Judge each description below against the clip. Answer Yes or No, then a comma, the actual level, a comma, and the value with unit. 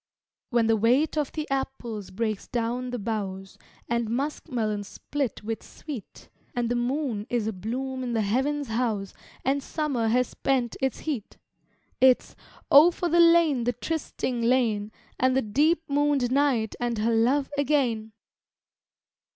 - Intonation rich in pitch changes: No, average, 3.9 semitones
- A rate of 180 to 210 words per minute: No, average, 150 wpm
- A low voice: No, high, 245 Hz